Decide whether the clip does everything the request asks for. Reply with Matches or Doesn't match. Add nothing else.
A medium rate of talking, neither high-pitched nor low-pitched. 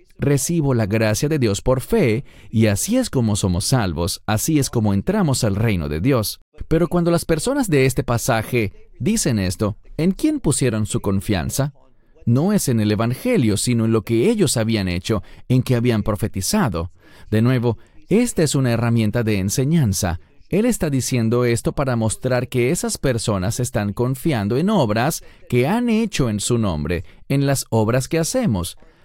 Doesn't match